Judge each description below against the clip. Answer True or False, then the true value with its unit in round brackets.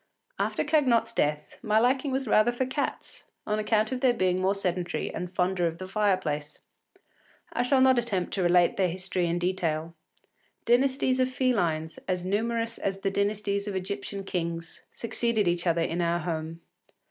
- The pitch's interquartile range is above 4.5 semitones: True (5.1 semitones)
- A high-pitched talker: True (195 Hz)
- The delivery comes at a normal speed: True (170 wpm)